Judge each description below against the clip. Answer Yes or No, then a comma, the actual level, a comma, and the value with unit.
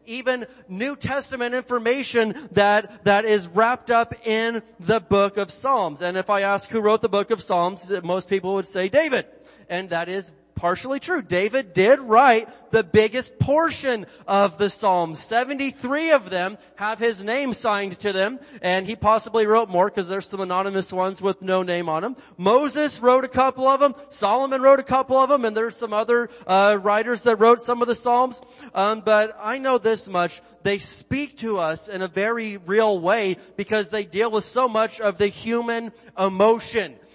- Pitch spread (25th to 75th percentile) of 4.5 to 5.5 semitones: No, average, 3.9 semitones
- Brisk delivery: No, average, 185 wpm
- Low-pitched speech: No, high, 220 Hz